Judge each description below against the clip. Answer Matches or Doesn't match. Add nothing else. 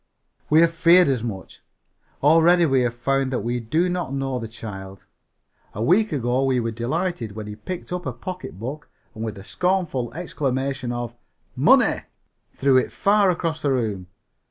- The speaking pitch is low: Matches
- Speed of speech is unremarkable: Matches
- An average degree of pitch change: Doesn't match